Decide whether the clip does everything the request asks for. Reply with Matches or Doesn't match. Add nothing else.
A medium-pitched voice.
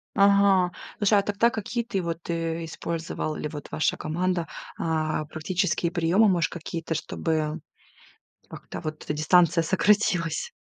Matches